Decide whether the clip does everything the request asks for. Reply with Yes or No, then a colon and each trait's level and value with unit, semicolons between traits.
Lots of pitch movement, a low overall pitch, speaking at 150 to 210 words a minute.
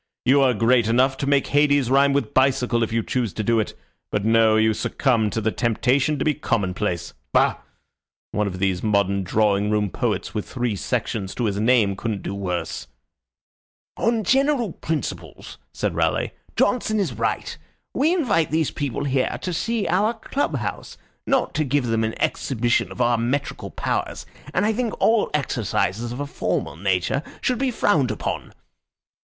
Yes: wide, 5.8 semitones; low, 125 Hz; average, 170 wpm